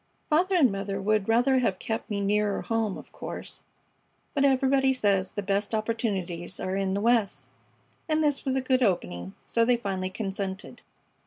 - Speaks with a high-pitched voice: Yes, high, 210 Hz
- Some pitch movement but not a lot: Yes, average, 4.6 semitones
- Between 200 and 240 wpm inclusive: No, average, 170 wpm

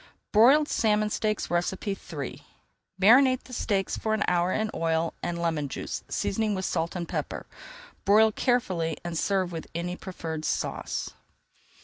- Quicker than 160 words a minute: No, average, 140 wpm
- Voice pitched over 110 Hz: Yes, high, 190 Hz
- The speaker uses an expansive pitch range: No, average, 4.3 semitones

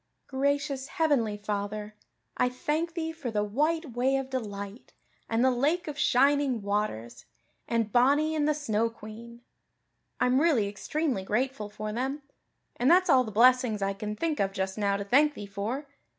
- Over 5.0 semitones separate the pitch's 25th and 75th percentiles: Yes, wide, 5.5 semitones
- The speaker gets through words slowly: No, average, 165 wpm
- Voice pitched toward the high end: Yes, high, 245 Hz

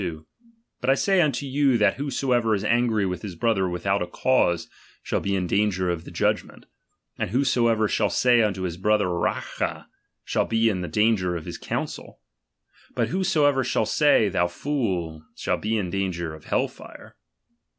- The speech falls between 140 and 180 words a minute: Yes, average, 175 wpm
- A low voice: Yes, low, 105 Hz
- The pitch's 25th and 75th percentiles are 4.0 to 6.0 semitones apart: Yes, average, 5.3 semitones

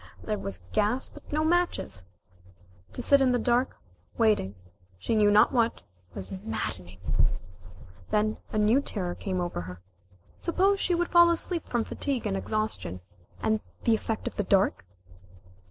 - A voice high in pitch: Yes, high, 220 Hz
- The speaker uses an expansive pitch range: Yes, wide, 5.8 semitones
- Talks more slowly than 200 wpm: Yes, average, 155 wpm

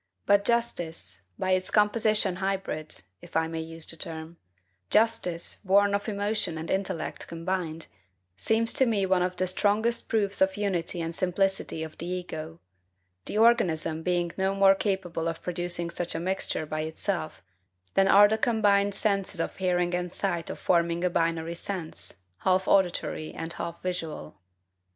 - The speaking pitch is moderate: Yes, medium, 180 Hz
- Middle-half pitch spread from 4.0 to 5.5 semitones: No, average, 3.2 semitones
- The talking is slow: No, average, 160 wpm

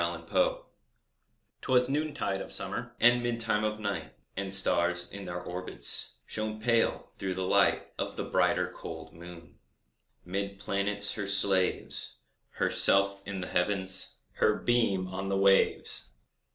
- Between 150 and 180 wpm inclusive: No, average, 140 wpm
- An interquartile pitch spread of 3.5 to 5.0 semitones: No, narrow, 2.5 semitones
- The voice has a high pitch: No, low, 100 Hz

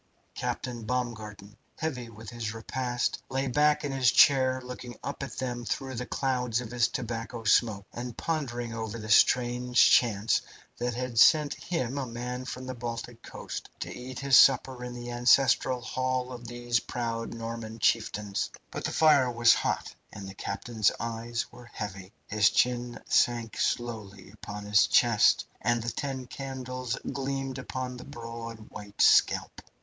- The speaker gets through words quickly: No, average, 160 wpm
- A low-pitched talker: Yes, low, 120 Hz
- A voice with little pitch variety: Yes, narrow, 2.0 semitones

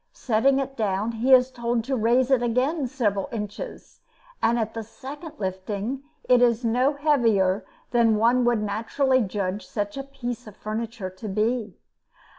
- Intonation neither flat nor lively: Yes, average, 3.4 semitones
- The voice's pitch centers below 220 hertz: No, high, 235 Hz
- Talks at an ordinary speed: Yes, average, 160 wpm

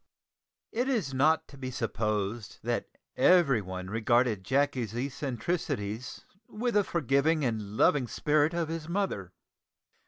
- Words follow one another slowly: Yes, slow, 120 wpm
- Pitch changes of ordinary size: No, wide, 6.6 semitones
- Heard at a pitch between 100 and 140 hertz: Yes, low, 135 Hz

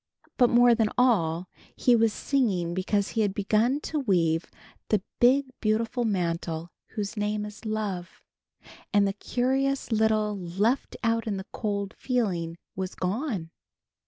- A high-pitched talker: Yes, high, 210 Hz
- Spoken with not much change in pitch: No, average, 4.1 semitones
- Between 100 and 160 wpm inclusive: Yes, average, 140 wpm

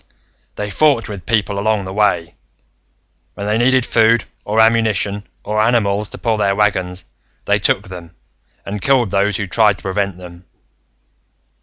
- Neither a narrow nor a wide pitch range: No, narrow, 2.3 semitones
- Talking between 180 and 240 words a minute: No, average, 155 wpm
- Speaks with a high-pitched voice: No, low, 105 Hz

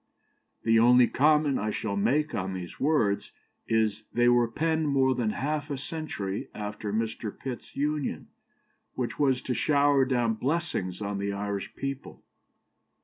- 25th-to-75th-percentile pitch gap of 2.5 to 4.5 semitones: No, average, 5.2 semitones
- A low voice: Yes, low, 120 Hz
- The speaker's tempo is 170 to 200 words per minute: No, average, 150 wpm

